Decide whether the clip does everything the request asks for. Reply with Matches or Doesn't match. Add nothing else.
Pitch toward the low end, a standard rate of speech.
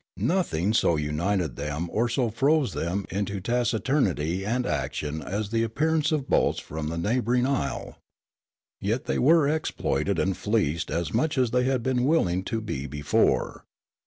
Matches